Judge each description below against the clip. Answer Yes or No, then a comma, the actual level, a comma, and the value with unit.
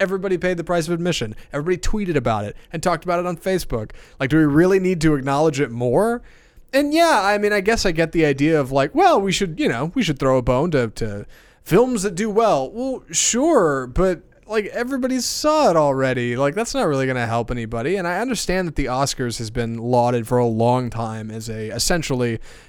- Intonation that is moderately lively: No, wide, 7.9 semitones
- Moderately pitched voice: Yes, medium, 160 Hz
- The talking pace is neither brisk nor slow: No, fast, 225 wpm